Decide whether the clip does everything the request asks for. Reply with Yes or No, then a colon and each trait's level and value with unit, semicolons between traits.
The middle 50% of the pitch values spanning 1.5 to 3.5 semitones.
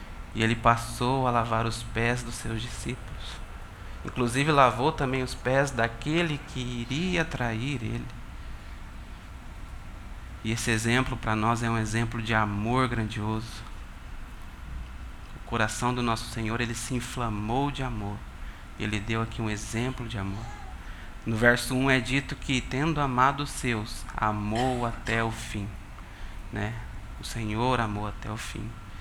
Yes: average, 3.2 semitones